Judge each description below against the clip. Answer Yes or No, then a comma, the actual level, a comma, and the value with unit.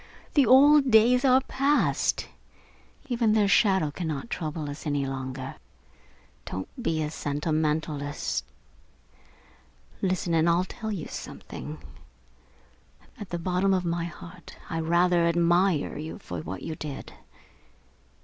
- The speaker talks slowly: Yes, slow, 120 wpm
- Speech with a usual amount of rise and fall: Yes, average, 4.7 semitones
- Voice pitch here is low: No, medium, 170 Hz